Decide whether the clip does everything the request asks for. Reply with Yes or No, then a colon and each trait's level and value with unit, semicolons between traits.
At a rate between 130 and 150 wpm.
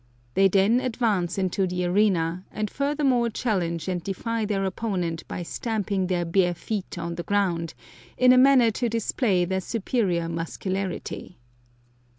Yes: average, 145 wpm